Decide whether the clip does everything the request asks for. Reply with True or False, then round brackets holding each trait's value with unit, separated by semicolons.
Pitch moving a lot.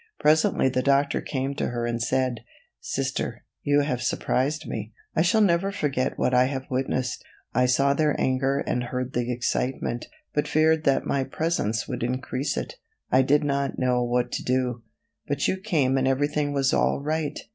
False (2.7 semitones)